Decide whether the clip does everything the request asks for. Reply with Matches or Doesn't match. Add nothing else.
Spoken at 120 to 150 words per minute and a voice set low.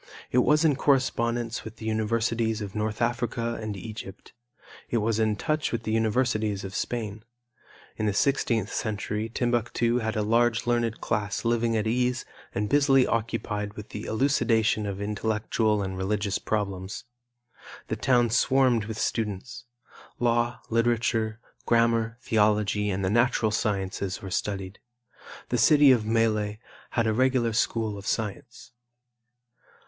Matches